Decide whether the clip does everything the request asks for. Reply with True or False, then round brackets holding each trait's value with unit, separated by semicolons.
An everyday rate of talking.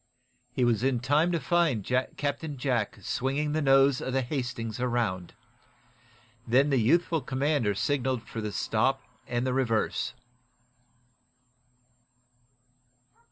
False (115 wpm)